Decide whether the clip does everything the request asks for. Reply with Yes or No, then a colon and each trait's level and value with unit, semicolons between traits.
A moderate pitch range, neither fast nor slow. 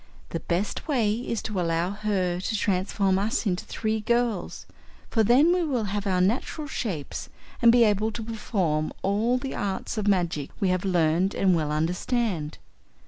Yes: average, 4.1 semitones; average, 170 wpm